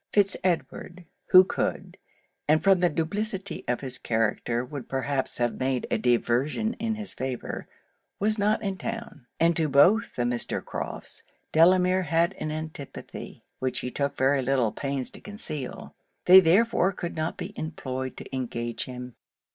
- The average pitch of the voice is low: No, medium, 155 Hz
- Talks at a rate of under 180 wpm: Yes, average, 155 wpm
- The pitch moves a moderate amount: No, wide, 6.4 semitones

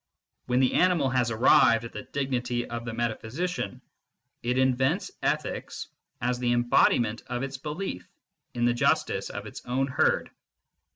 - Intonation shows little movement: Yes, narrow, 1.9 semitones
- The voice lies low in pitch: Yes, low, 125 Hz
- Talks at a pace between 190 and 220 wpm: No, average, 155 wpm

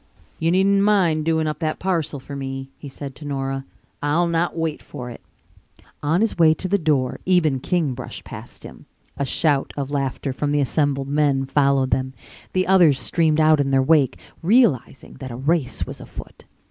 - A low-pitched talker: No, medium, 145 Hz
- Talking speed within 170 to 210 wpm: Yes, average, 185 wpm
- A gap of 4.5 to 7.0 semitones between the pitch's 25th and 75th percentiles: No, average, 3.5 semitones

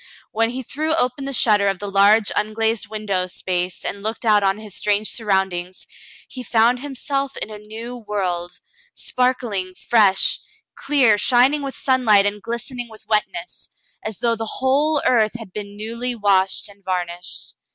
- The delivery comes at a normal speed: Yes, average, 160 wpm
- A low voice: No, high, 215 Hz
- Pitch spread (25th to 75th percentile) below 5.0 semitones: Yes, average, 3.7 semitones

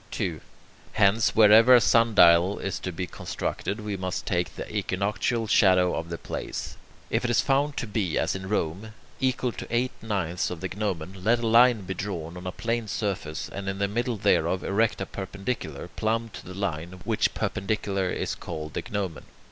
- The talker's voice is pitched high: No, low, 100 Hz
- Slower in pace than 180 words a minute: No, average, 190 wpm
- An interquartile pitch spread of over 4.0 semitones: No, average, 3.7 semitones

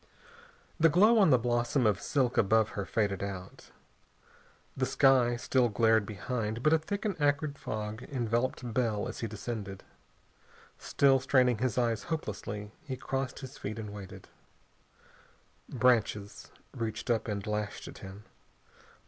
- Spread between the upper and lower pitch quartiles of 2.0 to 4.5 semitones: Yes, average, 3.8 semitones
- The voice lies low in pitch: Yes, low, 120 Hz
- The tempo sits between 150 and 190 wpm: No, average, 140 wpm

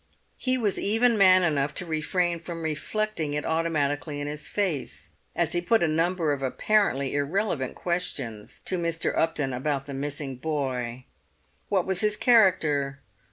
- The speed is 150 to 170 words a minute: Yes, average, 155 wpm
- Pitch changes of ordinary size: Yes, average, 4.5 semitones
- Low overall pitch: No, medium, 160 Hz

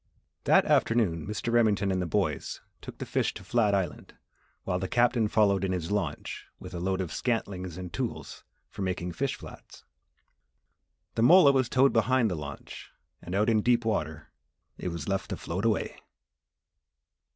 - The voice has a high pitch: No, low, 100 Hz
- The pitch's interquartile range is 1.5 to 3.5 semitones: No, average, 4.3 semitones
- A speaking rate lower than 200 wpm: Yes, average, 170 wpm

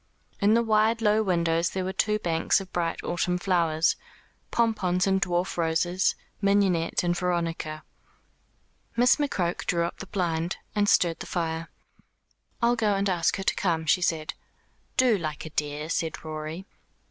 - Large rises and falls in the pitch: No, average, 3.3 semitones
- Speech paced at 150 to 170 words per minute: Yes, average, 160 wpm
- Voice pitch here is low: No, medium, 180 Hz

